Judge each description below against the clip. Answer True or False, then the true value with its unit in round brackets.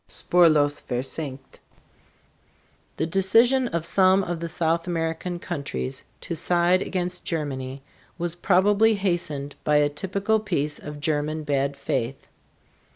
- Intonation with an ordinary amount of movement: True (4.0 semitones)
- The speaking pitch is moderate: True (165 Hz)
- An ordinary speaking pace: False (120 wpm)